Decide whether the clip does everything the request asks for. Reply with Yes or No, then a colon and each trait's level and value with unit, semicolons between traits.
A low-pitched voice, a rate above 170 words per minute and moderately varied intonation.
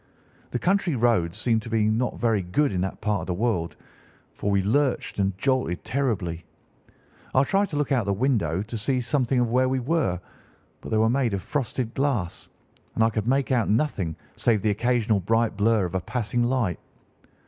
Yes: low, 115 Hz; average, 200 wpm; average, 4.5 semitones